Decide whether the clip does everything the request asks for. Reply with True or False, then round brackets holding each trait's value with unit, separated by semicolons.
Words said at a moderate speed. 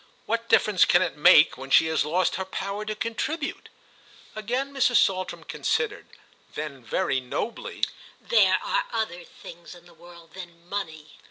True (155 wpm)